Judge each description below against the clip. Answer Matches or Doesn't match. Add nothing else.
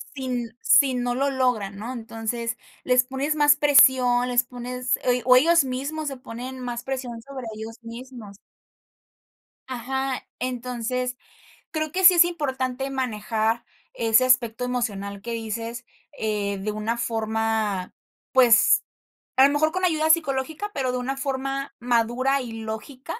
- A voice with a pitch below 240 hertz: Doesn't match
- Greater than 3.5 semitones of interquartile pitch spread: Doesn't match